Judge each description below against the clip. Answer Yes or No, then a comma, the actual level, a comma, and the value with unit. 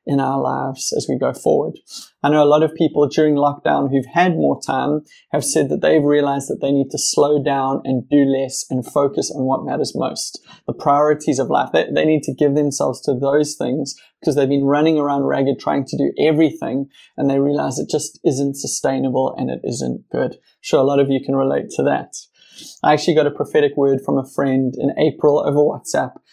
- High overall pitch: No, medium, 140 Hz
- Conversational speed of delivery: No, fast, 220 wpm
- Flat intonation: Yes, narrow, 1.5 semitones